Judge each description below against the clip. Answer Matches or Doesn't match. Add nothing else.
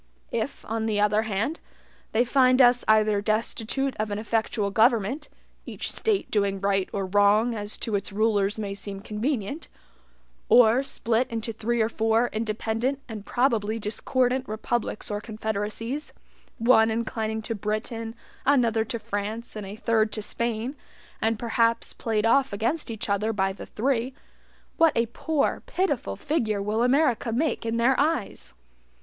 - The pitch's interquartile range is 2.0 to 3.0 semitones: Matches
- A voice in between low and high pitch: Doesn't match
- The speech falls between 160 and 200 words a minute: Doesn't match